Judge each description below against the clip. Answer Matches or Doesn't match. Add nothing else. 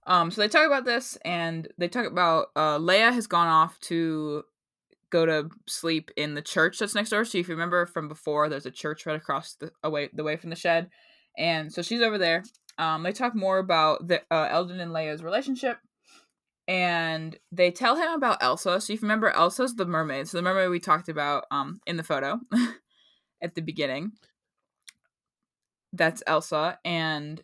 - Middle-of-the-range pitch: Matches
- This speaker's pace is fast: Doesn't match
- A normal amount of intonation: Matches